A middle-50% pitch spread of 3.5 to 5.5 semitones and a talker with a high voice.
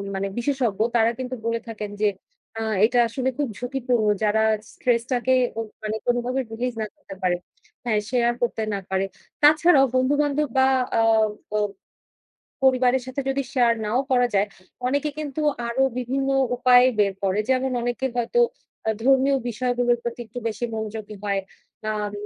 No: average, 3.0 semitones; high, 245 Hz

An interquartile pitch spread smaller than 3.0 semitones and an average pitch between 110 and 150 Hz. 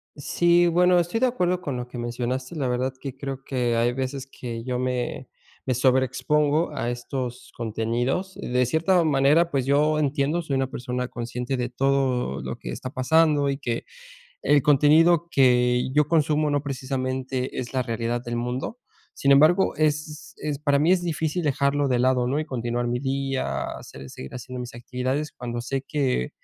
No: average, 3.4 semitones; low, 135 Hz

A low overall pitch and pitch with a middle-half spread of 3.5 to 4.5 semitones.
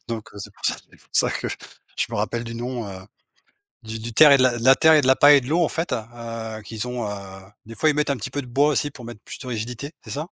Yes: low, 120 Hz; average, 4.0 semitones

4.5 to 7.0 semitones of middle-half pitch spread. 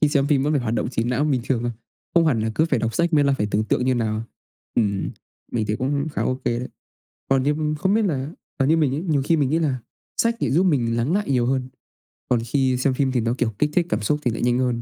No: average, 4.0 semitones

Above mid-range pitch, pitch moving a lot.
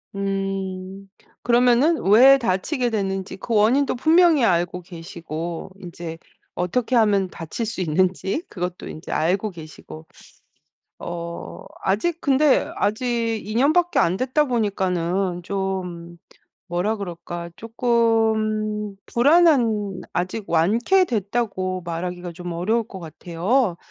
No: high, 195 Hz; average, 4.9 semitones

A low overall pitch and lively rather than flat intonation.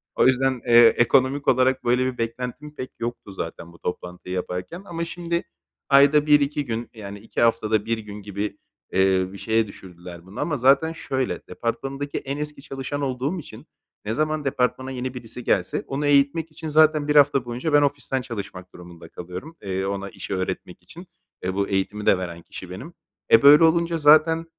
Yes: low, 125 Hz; wide, 6.4 semitones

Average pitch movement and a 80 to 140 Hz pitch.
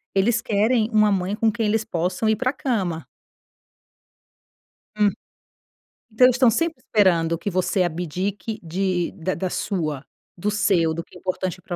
No: average, 3.7 semitones; high, 195 Hz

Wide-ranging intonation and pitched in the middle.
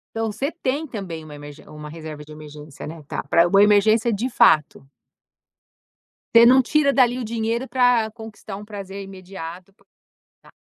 No: wide, 6.3 semitones; high, 205 Hz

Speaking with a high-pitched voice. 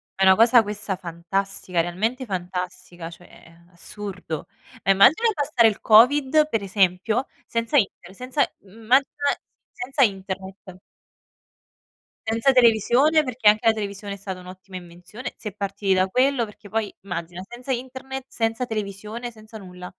Yes: high, 210 Hz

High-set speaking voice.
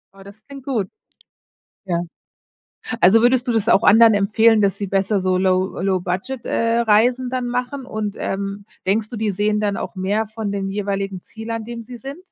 Yes: high, 215 Hz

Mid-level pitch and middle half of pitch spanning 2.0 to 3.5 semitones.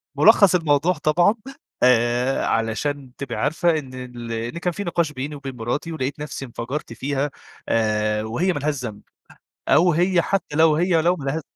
No: medium, 145 Hz; average, 5.1 semitones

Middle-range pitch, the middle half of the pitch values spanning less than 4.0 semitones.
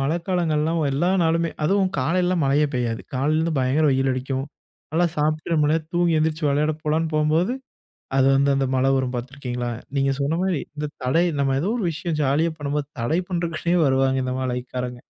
Yes: medium, 150 Hz; average, 3.6 semitones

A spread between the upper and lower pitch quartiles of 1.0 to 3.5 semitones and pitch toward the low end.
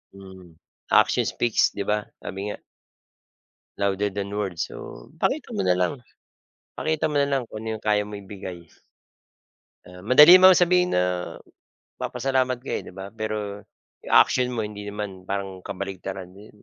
No: average, 4.7 semitones; low, 105 Hz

